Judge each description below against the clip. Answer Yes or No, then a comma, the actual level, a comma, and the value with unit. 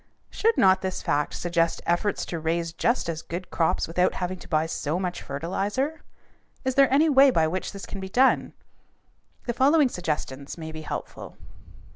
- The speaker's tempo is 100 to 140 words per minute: No, average, 175 wpm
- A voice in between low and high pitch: Yes, medium, 180 Hz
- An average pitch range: No, wide, 7.1 semitones